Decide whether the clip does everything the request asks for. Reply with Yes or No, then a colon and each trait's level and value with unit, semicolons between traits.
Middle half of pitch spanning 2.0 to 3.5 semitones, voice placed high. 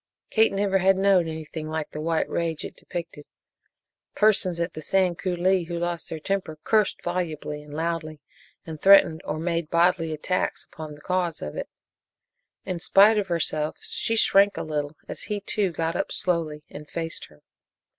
No: average, 3.1 semitones; medium, 170 Hz